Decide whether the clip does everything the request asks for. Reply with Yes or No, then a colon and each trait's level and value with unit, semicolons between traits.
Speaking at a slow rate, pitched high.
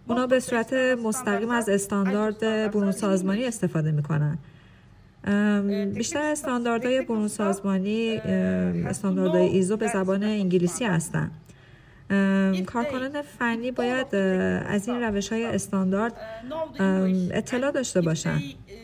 Yes: slow, 100 wpm; high, 205 Hz